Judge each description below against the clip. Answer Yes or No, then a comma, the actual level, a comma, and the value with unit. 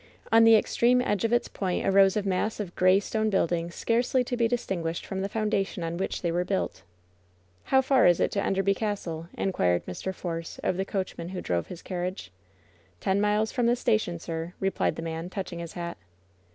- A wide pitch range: No, average, 3.9 semitones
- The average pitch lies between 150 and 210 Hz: Yes, high, 190 Hz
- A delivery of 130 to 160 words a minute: No, average, 200 wpm